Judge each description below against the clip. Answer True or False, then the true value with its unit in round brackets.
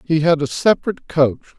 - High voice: False (160 Hz)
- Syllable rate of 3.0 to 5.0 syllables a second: False (6.2 syllables/s)